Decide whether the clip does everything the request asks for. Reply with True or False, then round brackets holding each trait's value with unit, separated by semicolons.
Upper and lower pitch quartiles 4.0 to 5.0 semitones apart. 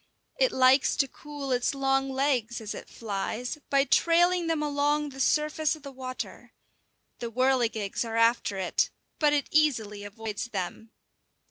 True (4.4 semitones)